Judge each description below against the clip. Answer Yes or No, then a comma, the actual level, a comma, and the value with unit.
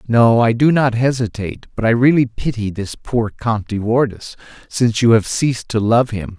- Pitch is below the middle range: Yes, low, 115 Hz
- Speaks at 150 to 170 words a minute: No, average, 195 wpm